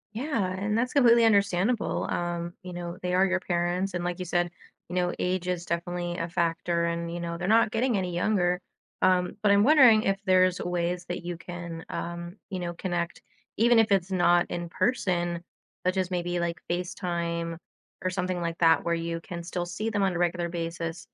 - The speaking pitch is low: No, medium, 175 Hz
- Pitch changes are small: Yes, narrow, 1.8 semitones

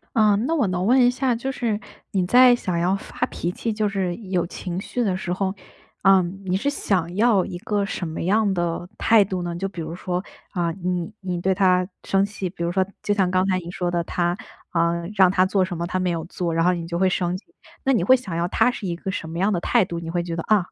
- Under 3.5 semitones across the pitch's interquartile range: Yes, narrow, 2.6 semitones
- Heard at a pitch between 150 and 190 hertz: Yes, medium, 185 Hz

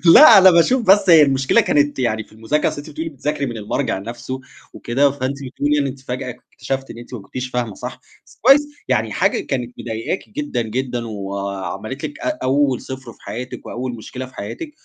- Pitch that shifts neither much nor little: Yes, average, 3.7 semitones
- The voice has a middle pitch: No, low, 130 Hz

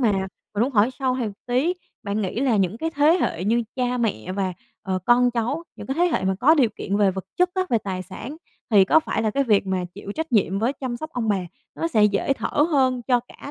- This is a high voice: Yes, high, 240 Hz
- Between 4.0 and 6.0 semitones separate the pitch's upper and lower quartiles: Yes, average, 5.2 semitones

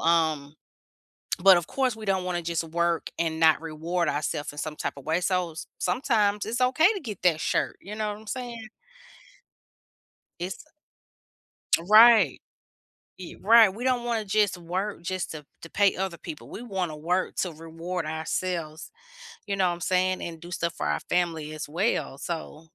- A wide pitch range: No, average, 4.2 semitones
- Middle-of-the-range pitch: Yes, medium, 180 Hz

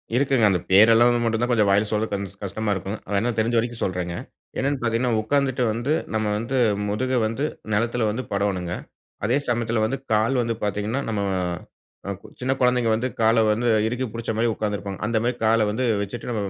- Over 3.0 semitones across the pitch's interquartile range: No, average, 2.7 semitones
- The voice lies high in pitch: No, low, 115 Hz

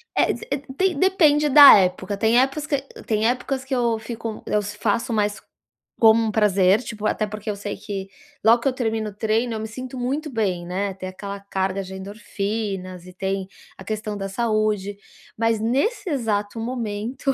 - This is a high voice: Yes, high, 215 Hz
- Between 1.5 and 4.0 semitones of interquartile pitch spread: Yes, average, 3.3 semitones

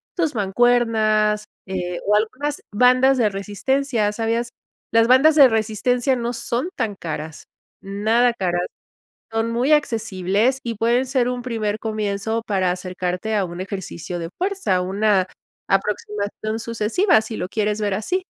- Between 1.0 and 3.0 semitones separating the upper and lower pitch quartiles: No, average, 3.6 semitones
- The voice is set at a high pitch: Yes, high, 220 Hz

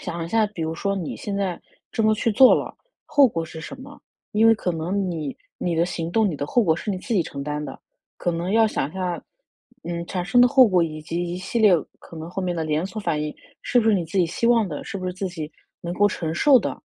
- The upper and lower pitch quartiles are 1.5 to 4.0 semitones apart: No, average, 4.6 semitones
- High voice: No, medium, 180 Hz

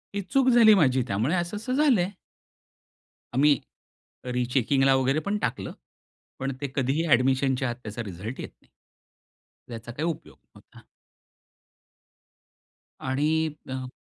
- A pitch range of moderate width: No, wide, 5.8 semitones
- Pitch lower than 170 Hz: Yes, low, 135 Hz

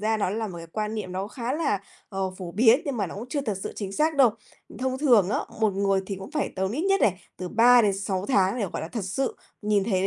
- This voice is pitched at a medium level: No, high, 210 Hz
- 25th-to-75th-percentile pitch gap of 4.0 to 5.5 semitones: Yes, average, 4.3 semitones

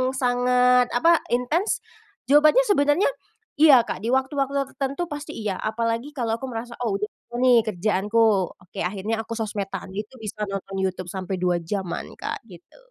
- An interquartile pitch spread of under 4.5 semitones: No, average, 5.0 semitones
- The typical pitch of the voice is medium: No, high, 230 Hz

